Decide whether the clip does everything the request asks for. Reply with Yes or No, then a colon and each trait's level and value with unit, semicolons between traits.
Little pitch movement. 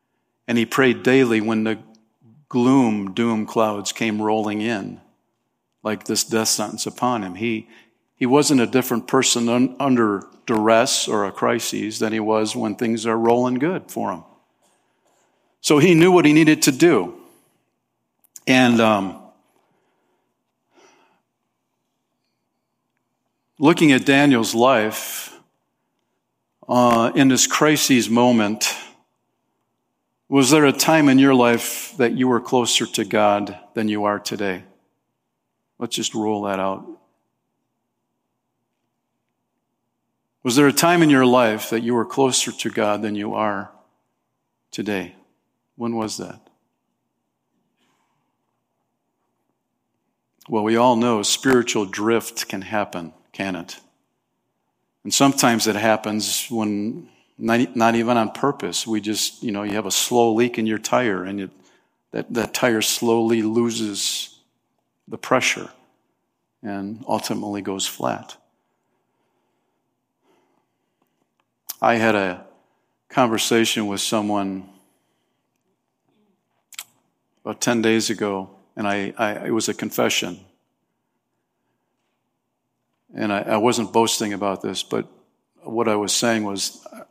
Yes: narrow, 2.3 semitones